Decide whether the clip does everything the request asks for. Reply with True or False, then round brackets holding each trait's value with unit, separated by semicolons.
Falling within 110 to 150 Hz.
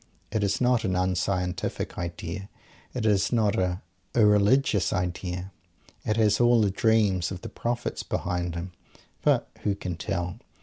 False (100 Hz)